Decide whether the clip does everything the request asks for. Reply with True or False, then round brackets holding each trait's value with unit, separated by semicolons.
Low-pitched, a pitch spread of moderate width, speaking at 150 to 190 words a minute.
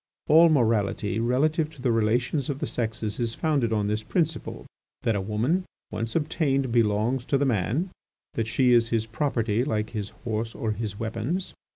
True (115 Hz; 4.1 semitones; 175 wpm)